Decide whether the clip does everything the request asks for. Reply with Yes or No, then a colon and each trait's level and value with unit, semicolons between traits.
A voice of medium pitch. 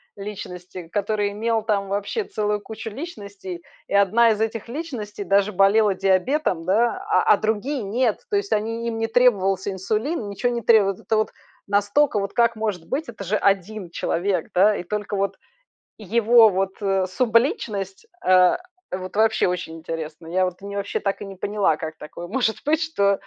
No: high, 205 Hz